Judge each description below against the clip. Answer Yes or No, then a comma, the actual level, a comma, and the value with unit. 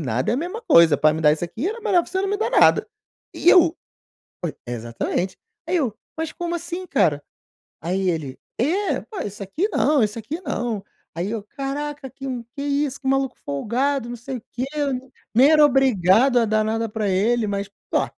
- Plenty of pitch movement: Yes, wide, 7.0 semitones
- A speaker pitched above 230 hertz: Yes, high, 245 Hz